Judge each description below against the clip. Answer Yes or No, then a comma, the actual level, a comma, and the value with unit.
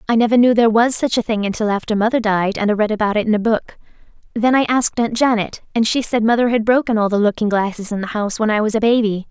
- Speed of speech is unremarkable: No, fast, 275 wpm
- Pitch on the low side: No, high, 220 Hz